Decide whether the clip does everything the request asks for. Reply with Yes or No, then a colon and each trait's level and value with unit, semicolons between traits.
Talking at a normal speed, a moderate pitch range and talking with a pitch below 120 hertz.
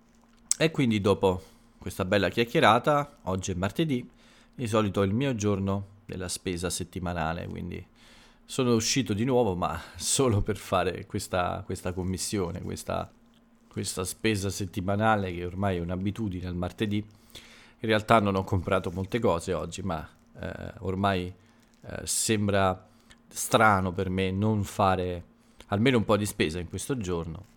Yes: average, 145 wpm; average, 3.7 semitones; low, 100 Hz